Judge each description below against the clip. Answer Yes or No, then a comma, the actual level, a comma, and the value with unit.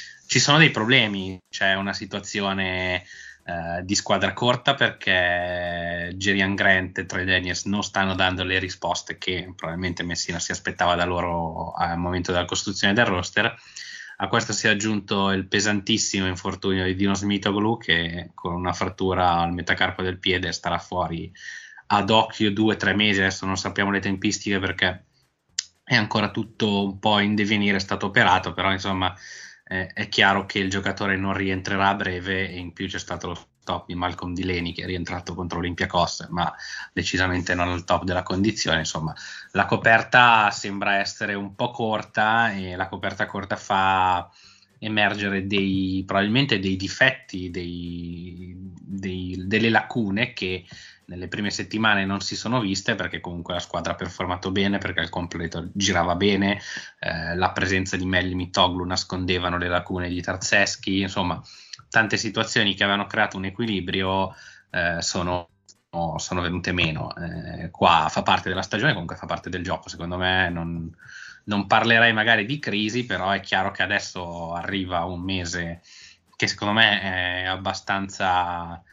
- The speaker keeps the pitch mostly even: Yes, narrow, 2.2 semitones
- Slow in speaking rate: No, average, 160 wpm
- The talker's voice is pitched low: Yes, very low, 95 Hz